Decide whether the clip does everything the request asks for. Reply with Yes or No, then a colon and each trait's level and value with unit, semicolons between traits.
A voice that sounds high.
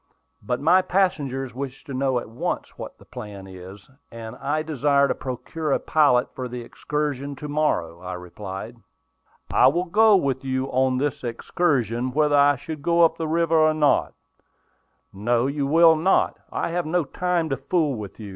No: medium, 140 Hz